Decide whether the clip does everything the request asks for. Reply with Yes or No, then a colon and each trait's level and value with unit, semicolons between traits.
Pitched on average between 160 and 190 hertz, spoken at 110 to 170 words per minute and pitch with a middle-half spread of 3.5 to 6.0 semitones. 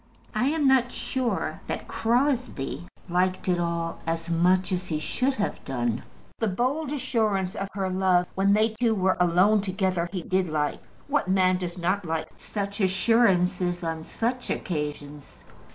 Yes: medium, 185 Hz; average, 155 wpm; average, 4.2 semitones